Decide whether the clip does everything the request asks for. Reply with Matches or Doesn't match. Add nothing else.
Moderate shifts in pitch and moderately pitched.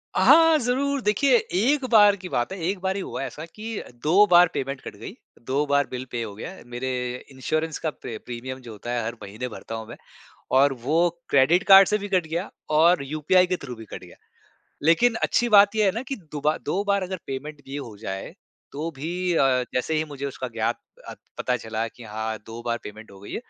Doesn't match